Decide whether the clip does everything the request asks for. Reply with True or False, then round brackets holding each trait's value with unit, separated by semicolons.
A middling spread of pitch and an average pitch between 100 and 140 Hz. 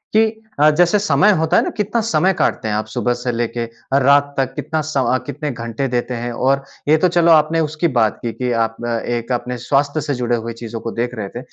True (4.7 semitones; 135 Hz)